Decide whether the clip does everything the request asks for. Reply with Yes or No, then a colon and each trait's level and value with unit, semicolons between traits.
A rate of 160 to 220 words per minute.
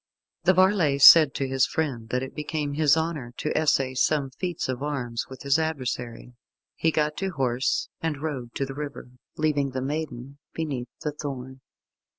Yes: average, 170 wpm